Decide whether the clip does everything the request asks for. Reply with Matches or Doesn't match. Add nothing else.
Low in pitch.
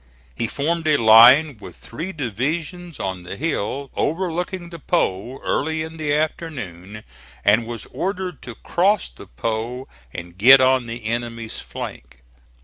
Matches